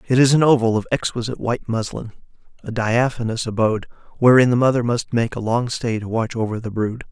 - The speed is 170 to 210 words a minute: Yes, average, 200 wpm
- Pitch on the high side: No, low, 115 Hz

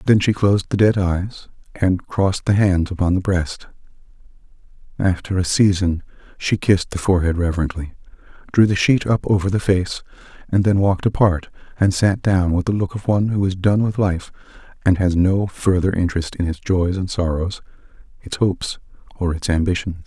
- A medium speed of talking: Yes, average, 180 wpm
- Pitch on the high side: No, very low, 95 Hz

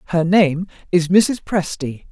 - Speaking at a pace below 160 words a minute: Yes, average, 140 wpm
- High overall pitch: No, medium, 175 Hz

